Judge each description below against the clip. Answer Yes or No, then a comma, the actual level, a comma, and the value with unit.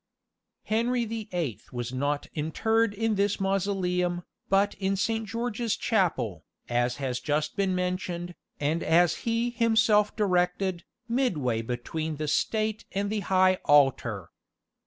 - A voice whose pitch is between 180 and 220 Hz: Yes, medium, 185 Hz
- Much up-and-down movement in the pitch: Yes, wide, 6.1 semitones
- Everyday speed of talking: No, slow, 130 wpm